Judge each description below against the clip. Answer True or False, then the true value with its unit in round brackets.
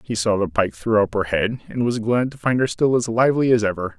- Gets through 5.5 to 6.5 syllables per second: True (5.8 syllables/s)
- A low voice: True (115 Hz)